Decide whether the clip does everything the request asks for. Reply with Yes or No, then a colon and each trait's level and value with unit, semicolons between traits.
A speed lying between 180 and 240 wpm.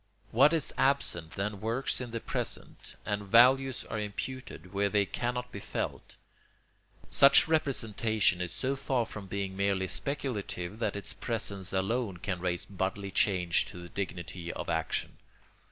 No: average, 150 wpm